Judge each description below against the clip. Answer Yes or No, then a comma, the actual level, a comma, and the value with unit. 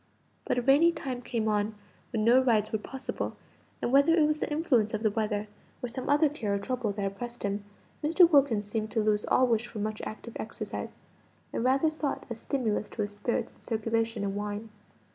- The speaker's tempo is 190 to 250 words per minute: Yes, fast, 205 wpm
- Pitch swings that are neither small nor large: Yes, average, 4.0 semitones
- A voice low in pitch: No, high, 230 Hz